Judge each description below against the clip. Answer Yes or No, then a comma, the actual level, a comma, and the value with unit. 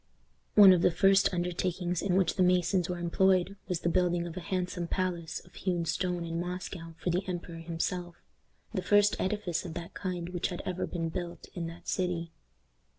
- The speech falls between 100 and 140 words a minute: No, average, 190 wpm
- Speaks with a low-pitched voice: No, medium, 180 Hz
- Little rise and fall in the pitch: Yes, narrow, 1.3 semitones